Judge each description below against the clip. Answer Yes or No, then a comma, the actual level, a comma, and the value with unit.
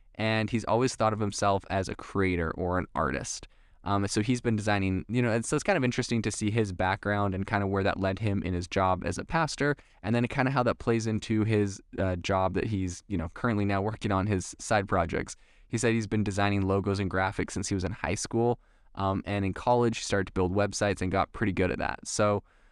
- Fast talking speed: Yes, fast, 250 wpm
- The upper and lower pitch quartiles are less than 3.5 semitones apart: Yes, average, 2.8 semitones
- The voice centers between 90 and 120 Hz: Yes, low, 100 Hz